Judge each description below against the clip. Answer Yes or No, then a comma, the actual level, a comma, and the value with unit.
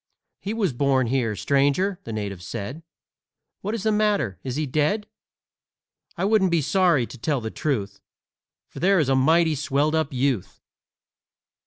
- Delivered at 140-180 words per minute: Yes, average, 160 wpm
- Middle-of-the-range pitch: Yes, medium, 145 Hz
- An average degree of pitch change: No, wide, 6.5 semitones